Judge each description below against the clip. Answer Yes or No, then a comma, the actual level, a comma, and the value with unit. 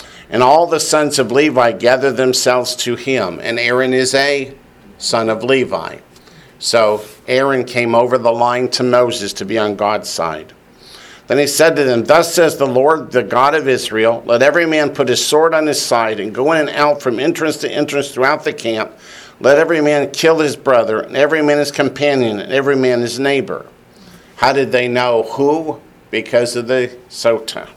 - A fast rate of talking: No, average, 190 wpm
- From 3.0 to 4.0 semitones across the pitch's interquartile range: Yes, average, 3.3 semitones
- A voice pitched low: Yes, low, 130 Hz